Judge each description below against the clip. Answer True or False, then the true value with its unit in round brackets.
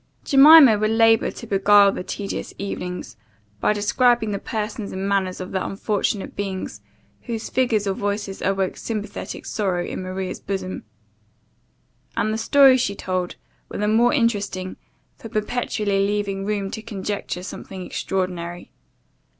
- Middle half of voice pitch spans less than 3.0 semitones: True (2.4 semitones)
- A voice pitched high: True (205 Hz)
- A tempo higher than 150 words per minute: False (140 wpm)